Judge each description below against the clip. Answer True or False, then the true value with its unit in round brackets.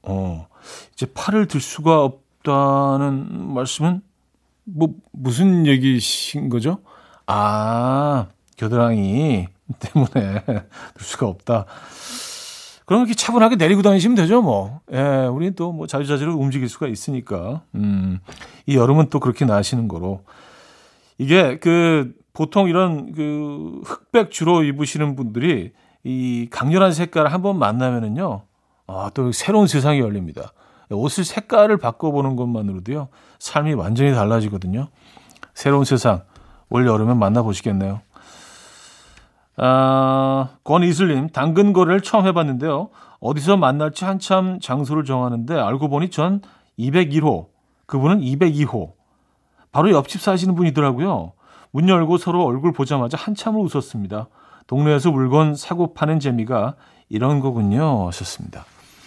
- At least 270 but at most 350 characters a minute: True (275 characters per minute)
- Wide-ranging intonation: True (6.2 semitones)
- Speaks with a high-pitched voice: False (140 Hz)